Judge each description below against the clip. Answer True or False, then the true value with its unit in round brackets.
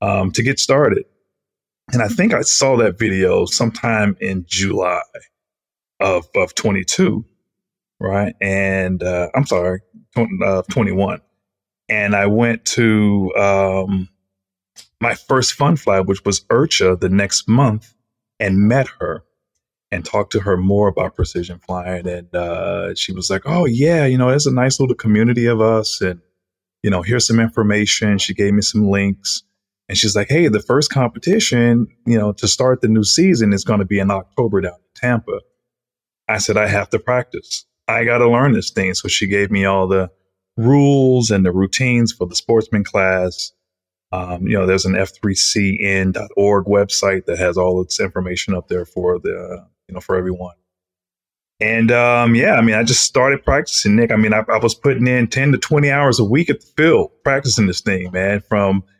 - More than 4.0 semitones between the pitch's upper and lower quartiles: False (3.7 semitones)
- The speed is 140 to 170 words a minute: False (180 wpm)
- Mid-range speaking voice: False (100 Hz)